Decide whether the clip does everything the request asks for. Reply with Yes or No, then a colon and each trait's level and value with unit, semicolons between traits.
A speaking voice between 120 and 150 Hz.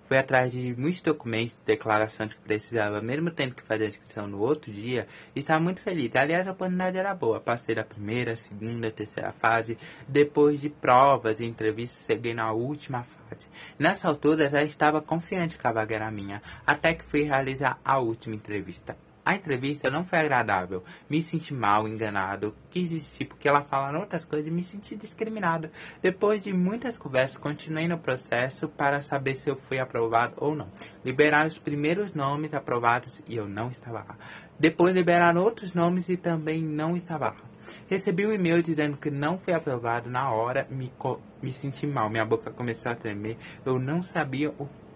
Yes: medium, 140 Hz